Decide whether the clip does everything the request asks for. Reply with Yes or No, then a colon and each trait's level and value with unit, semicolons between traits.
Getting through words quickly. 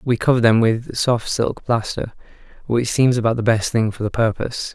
Yes: fast, 215 wpm